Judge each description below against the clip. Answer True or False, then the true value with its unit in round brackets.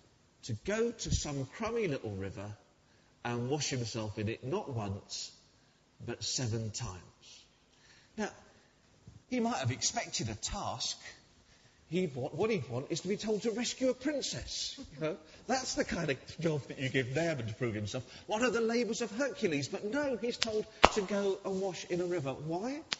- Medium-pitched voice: True (155 Hz)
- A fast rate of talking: False (180 wpm)